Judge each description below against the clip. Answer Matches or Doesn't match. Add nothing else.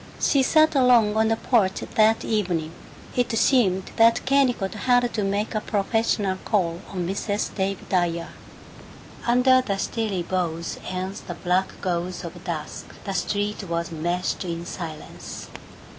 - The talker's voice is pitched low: Doesn't match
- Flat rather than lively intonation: Doesn't match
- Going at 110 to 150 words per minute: Matches